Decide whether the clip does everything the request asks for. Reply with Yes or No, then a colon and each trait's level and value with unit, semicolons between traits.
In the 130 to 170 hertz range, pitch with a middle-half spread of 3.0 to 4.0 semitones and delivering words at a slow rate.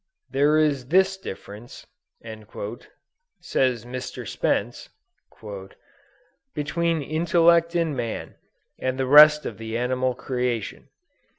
No: low, 135 Hz; average, 5.2 semitones; slow, 95 wpm